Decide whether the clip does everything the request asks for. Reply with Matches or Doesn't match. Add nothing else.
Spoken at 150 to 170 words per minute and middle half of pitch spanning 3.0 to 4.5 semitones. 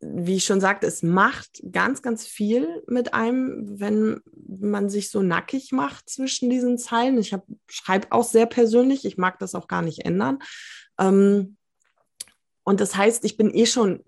Matches